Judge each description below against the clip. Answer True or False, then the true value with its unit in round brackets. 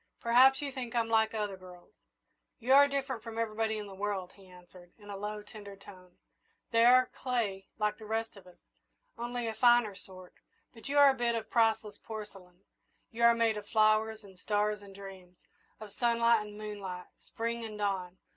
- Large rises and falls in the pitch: False (2.9 semitones)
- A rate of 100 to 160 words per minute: False (195 wpm)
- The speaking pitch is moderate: False (215 Hz)